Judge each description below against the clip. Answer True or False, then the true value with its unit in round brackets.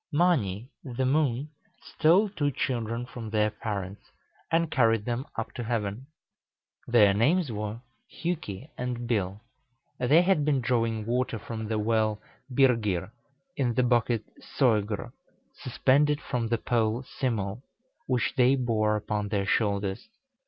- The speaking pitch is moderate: False (115 Hz)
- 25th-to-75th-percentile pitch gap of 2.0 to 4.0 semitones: True (3.5 semitones)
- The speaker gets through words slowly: True (130 wpm)